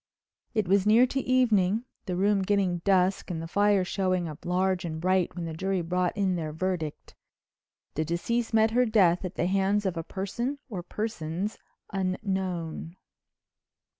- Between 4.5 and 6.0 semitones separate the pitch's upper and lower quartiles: No, average, 2.8 semitones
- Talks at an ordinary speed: Yes, average, 165 wpm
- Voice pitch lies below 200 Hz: Yes, high, 190 Hz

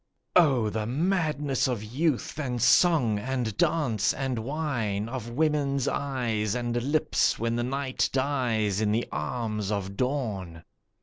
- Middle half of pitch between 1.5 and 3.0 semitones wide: No, average, 4.6 semitones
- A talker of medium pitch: No, low, 125 Hz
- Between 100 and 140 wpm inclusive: Yes, slow, 135 wpm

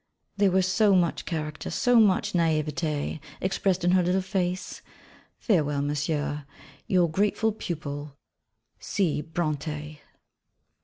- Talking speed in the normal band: No, slow, 110 wpm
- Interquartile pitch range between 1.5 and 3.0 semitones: No, average, 3.9 semitones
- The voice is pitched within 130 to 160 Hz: No, medium, 170 Hz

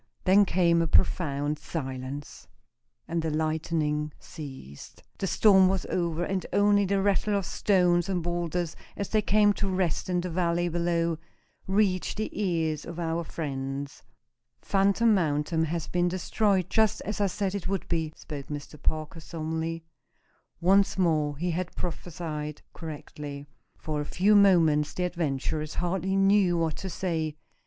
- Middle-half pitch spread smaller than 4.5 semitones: Yes, average, 3.6 semitones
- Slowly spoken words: No, average, 150 wpm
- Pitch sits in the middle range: Yes, medium, 170 Hz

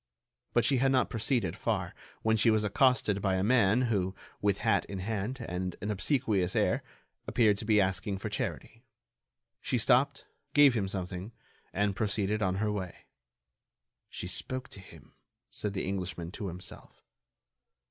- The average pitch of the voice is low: Yes, low, 105 Hz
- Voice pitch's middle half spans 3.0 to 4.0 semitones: Yes, average, 3.6 semitones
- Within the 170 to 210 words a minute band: No, average, 160 wpm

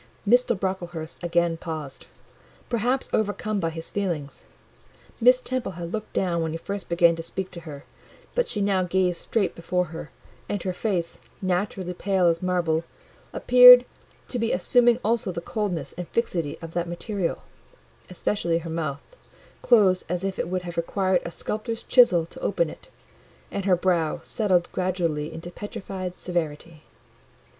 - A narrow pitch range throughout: No, average, 3.4 semitones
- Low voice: No, medium, 180 Hz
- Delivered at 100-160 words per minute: Yes, average, 155 wpm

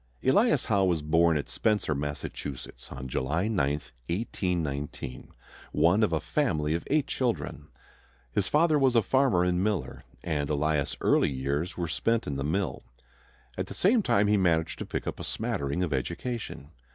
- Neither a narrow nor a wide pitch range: No, wide, 6.3 semitones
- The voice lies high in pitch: No, very low, 85 Hz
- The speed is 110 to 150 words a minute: No, average, 165 wpm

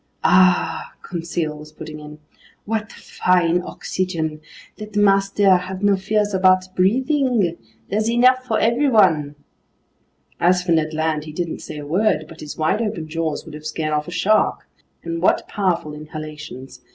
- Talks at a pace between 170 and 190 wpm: No, average, 150 wpm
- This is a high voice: No, medium, 180 Hz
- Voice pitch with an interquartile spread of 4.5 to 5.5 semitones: Yes, average, 4.8 semitones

